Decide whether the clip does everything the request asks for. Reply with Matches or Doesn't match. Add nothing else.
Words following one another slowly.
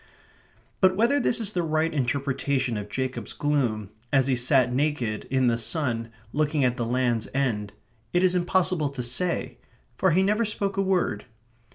Doesn't match